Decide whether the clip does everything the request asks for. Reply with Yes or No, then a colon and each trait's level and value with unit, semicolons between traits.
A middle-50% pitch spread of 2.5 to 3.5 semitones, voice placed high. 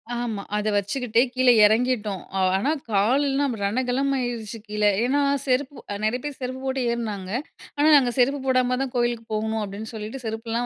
Yes: average, 3.1 semitones; high, 240 Hz